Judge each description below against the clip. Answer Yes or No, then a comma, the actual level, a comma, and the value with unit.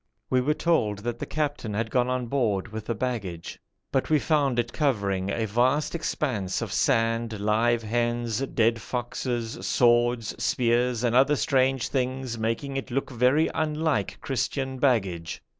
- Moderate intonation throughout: Yes, average, 3.0 semitones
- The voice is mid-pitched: No, low, 120 Hz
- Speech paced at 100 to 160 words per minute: Yes, average, 155 wpm